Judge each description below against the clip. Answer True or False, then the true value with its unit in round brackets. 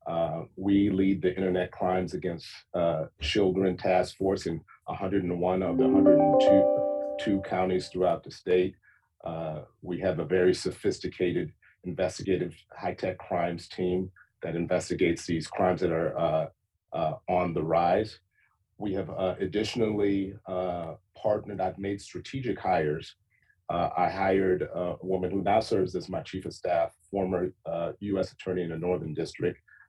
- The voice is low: True (95 Hz)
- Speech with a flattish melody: True (1.7 semitones)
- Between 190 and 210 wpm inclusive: False (150 wpm)